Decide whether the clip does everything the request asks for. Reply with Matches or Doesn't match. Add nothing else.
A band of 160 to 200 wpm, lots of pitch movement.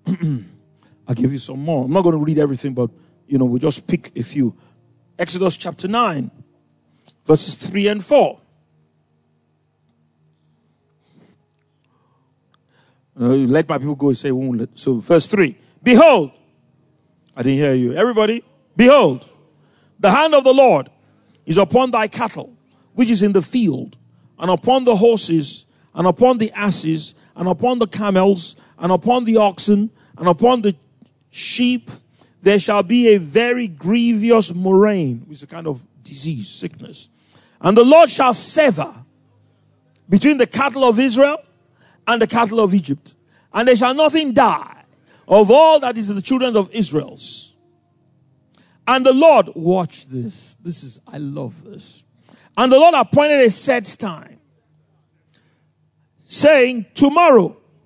Doesn't match